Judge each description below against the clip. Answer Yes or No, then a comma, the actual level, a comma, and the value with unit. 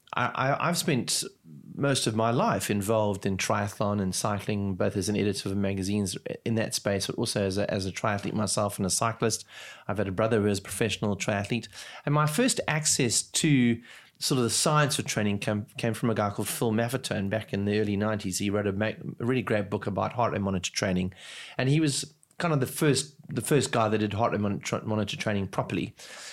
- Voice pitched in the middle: No, low, 110 Hz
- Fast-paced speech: Yes, fast, 215 wpm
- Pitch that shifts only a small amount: No, average, 3.9 semitones